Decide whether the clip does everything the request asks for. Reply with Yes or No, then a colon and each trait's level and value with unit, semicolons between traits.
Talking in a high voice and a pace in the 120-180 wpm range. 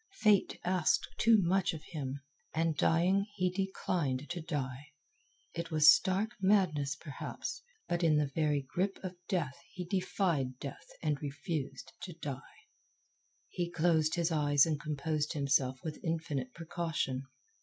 No: medium, 160 Hz; average, 140 wpm